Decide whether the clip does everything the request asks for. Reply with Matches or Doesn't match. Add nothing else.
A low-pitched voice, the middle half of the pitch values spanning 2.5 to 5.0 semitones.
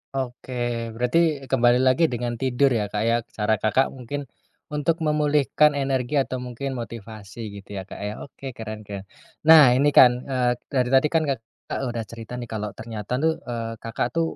Matches